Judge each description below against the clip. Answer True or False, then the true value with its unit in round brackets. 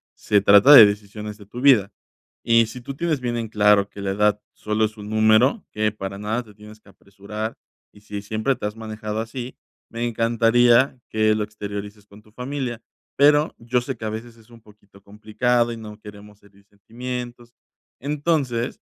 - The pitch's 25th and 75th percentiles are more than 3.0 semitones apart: False (2.5 semitones)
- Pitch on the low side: True (110 Hz)